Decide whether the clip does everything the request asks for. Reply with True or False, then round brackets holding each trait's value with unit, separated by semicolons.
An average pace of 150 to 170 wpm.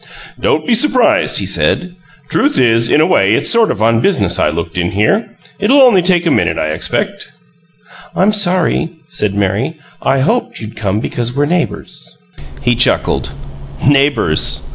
True (165 wpm)